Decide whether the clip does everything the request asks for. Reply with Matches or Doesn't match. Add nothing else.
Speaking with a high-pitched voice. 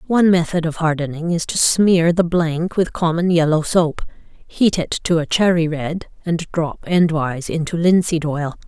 Doesn't match